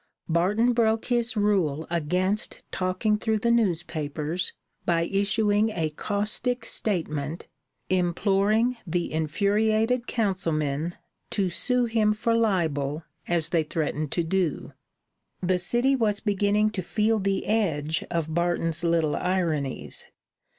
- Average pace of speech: No, slow, 115 wpm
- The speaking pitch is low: No, high, 190 Hz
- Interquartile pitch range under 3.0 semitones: No, average, 4.7 semitones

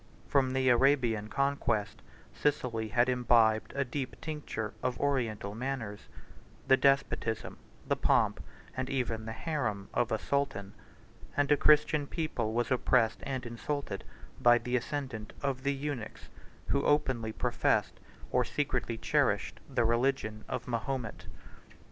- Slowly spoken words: Yes, slow, 130 wpm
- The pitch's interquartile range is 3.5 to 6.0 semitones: Yes, average, 3.8 semitones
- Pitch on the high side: No, low, 125 Hz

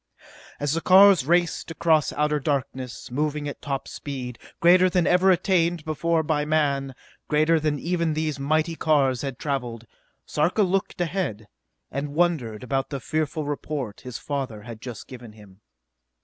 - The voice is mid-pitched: Yes, medium, 150 Hz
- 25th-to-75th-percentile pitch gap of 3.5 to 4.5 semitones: Yes, average, 3.8 semitones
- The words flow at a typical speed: Yes, average, 150 wpm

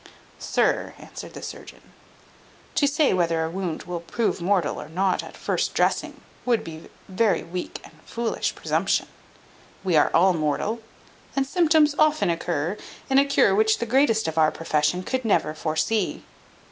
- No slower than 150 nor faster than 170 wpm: Yes, average, 160 wpm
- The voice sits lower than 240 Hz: Yes, high, 190 Hz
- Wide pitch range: Yes, wide, 6.2 semitones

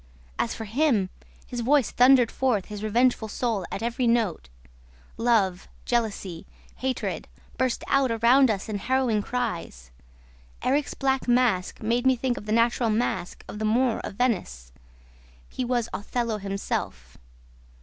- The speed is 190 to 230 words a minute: No, average, 140 wpm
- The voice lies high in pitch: Yes, high, 230 Hz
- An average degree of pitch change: Yes, average, 3.6 semitones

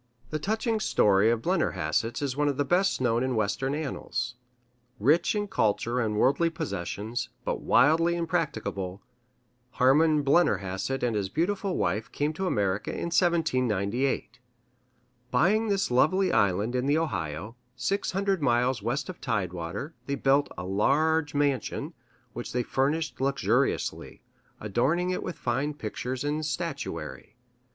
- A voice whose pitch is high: No, low, 135 Hz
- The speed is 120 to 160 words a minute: Yes, average, 140 wpm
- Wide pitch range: Yes, wide, 6.5 semitones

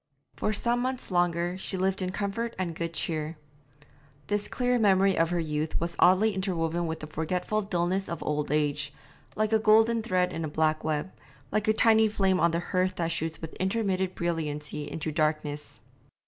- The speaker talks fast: No, average, 180 wpm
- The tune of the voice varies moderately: Yes, average, 4.0 semitones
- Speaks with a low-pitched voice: No, medium, 180 Hz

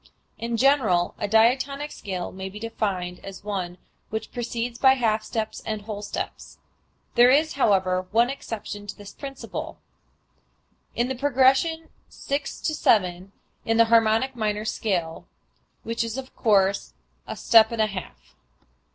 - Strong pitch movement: No, average, 4.0 semitones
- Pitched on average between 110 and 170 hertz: No, high, 220 Hz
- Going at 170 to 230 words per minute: No, average, 150 wpm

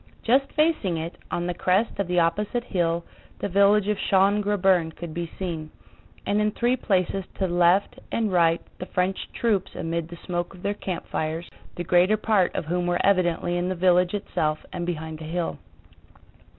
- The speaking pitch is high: No, medium, 180 Hz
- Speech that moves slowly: No, average, 180 wpm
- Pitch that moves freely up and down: No, average, 2.8 semitones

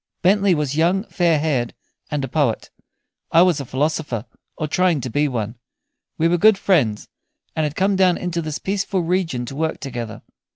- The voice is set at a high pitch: No, medium, 155 Hz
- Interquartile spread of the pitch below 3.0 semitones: No, average, 5.0 semitones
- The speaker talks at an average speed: Yes, average, 180 wpm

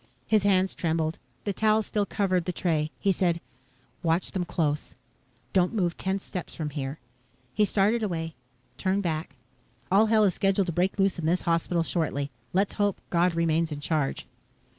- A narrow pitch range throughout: No, average, 3.2 semitones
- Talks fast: No, average, 170 wpm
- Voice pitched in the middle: Yes, medium, 180 Hz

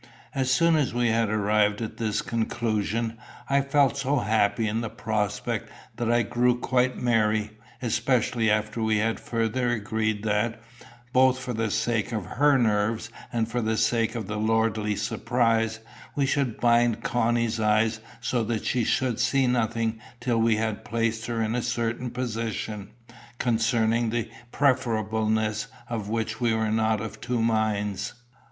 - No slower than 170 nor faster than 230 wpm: No, average, 155 wpm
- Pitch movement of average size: No, narrow, 1.8 semitones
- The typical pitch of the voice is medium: No, low, 115 Hz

